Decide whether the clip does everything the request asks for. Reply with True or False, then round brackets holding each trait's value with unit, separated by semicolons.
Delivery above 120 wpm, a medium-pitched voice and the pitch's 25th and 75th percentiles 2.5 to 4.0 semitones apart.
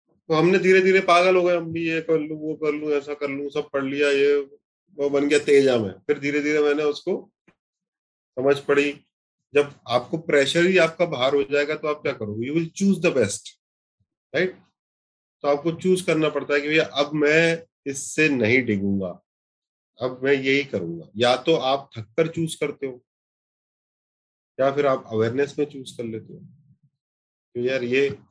True (185 wpm; 145 Hz; 3.1 semitones)